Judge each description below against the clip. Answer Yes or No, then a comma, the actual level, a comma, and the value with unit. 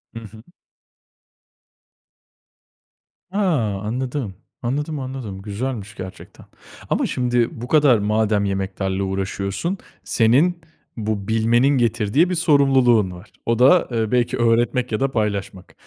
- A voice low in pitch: Yes, low, 115 Hz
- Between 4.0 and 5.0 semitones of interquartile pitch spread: Yes, average, 4.3 semitones